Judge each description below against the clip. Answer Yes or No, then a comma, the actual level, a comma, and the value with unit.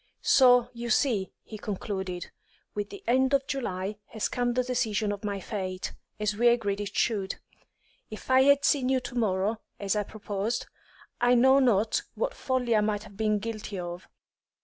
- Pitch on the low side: No, high, 215 Hz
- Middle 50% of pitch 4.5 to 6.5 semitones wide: No, average, 3.5 semitones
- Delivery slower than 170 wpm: No, average, 175 wpm